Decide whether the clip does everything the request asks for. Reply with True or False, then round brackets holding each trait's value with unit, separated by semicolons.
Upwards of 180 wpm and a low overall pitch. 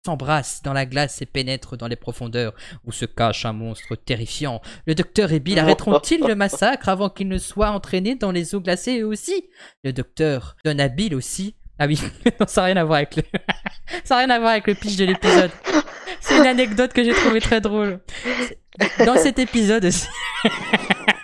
False (195 wpm; 190 Hz)